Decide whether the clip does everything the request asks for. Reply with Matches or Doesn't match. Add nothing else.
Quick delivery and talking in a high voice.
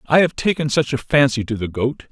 Doesn't match